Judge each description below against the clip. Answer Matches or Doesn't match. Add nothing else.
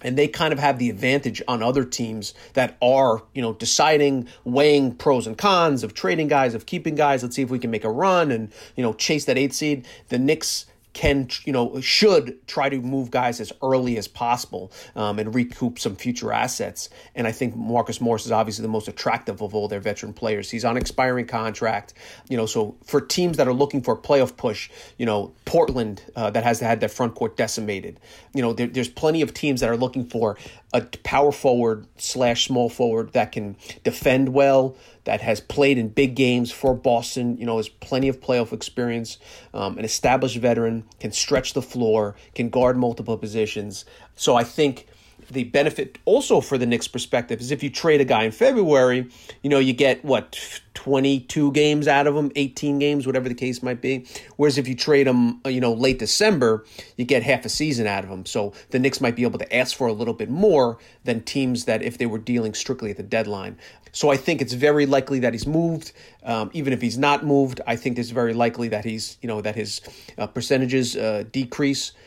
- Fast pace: Matches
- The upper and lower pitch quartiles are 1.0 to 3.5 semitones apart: Matches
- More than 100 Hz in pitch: Matches